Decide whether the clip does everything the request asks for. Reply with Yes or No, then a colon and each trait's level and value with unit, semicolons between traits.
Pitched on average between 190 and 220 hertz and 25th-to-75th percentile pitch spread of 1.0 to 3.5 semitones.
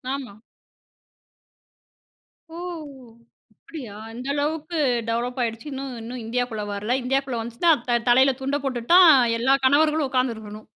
No: very high, 255 Hz; average, 3.1 semitones